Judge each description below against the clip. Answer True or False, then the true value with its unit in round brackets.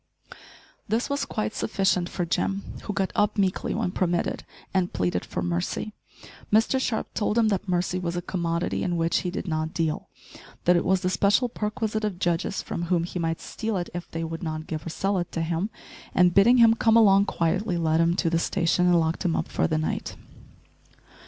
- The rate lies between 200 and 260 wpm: True (205 wpm)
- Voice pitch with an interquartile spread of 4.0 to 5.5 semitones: False (3.6 semitones)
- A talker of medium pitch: True (180 Hz)